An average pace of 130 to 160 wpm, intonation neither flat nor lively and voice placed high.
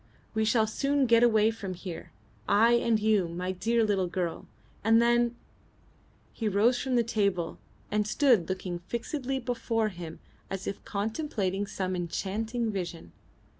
Yes: average, 150 wpm; average, 3.9 semitones; high, 215 Hz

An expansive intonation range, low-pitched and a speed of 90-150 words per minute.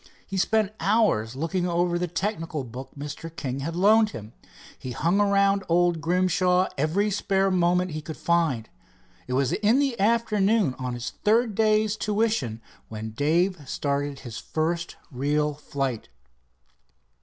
No: wide, 6.0 semitones; medium, 170 Hz; average, 140 wpm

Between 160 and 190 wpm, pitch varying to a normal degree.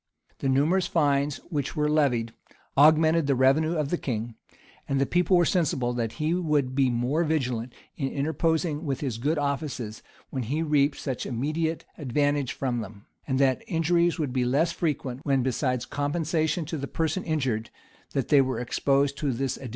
Yes: average, 180 wpm; average, 3.4 semitones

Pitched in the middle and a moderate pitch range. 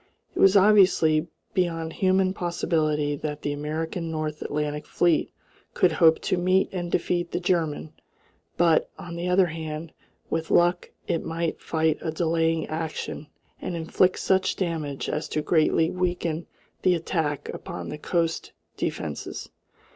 No: medium, 165 Hz; narrow, 2.2 semitones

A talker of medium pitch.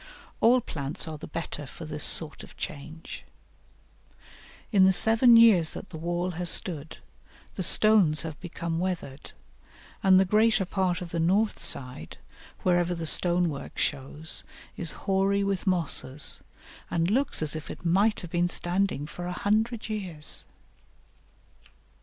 Yes: medium, 175 Hz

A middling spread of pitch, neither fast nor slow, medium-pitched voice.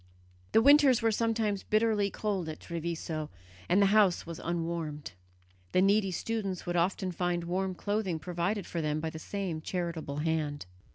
Yes: average, 3.8 semitones; average, 160 wpm; medium, 180 Hz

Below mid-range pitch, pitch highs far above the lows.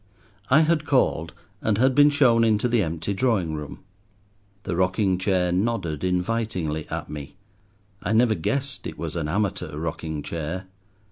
Yes: very low, 95 Hz; wide, 6.0 semitones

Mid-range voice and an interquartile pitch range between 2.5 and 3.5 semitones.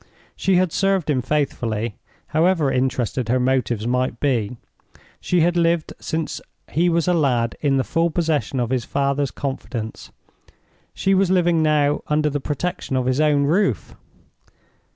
No: medium, 145 Hz; average, 4.6 semitones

